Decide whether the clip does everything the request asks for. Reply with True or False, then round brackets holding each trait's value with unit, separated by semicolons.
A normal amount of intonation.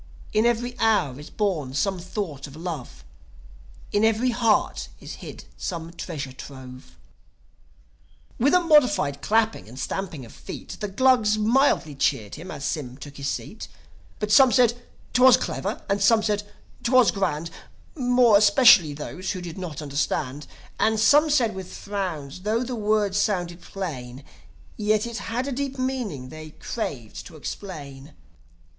False (7.4 semitones)